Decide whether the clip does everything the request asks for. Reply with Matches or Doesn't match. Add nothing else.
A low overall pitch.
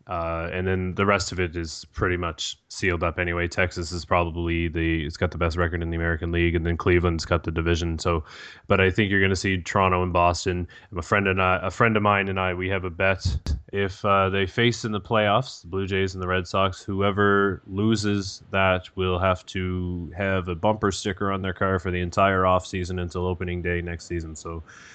Matches